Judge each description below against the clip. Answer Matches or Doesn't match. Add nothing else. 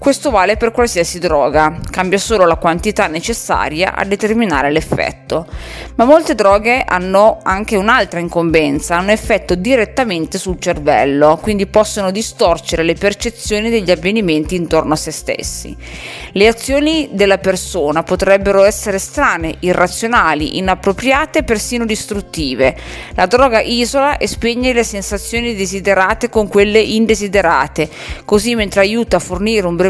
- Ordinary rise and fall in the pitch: Matches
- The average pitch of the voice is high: Matches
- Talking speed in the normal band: Matches